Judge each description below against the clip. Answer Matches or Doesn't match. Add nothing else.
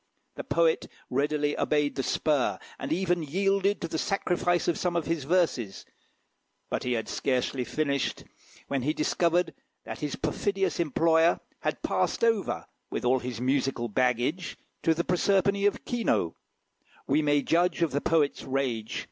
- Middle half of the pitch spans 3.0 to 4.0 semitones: Doesn't match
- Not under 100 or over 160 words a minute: Matches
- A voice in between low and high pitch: Matches